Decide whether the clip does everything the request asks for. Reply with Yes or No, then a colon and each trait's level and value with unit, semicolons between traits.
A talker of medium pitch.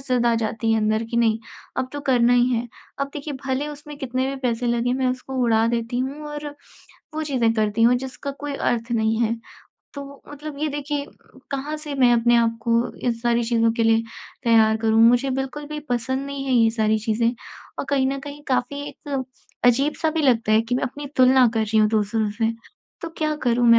No: high, 245 Hz